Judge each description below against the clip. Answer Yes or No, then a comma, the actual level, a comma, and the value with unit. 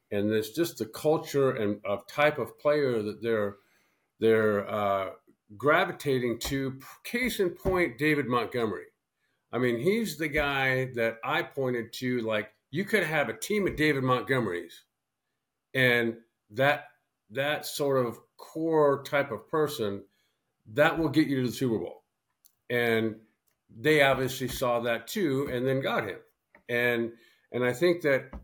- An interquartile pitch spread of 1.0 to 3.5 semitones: No, average, 4.6 semitones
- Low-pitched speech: Yes, low, 130 Hz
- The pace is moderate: Yes, average, 150 wpm